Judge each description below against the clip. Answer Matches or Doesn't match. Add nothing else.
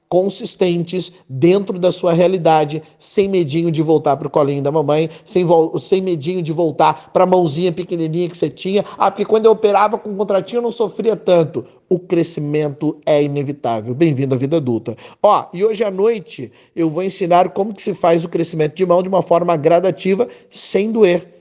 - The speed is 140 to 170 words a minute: Doesn't match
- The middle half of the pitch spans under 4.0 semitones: Matches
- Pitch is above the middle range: Doesn't match